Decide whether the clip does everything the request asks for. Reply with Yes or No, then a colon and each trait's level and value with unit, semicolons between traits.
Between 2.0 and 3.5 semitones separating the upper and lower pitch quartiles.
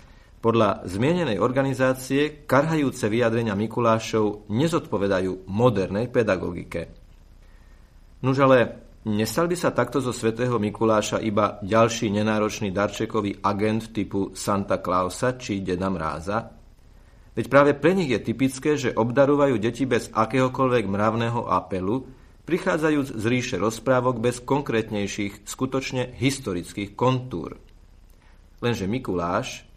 No: average, 4.4 semitones